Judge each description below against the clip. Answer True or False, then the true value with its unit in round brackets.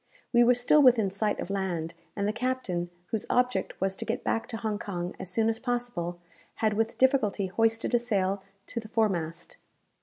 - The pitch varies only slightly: False (4.0 semitones)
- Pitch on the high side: True (220 Hz)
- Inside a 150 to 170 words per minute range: False (190 wpm)